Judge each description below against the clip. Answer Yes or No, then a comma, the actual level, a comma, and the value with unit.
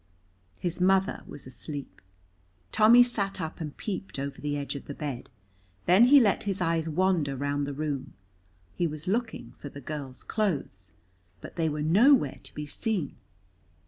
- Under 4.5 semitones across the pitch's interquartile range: No, wide, 5.4 semitones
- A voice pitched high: No, medium, 160 Hz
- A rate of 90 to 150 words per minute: No, average, 165 wpm